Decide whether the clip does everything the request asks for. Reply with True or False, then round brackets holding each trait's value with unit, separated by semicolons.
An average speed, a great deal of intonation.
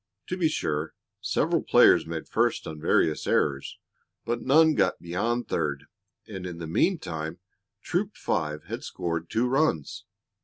True (145 wpm; 8.1 semitones)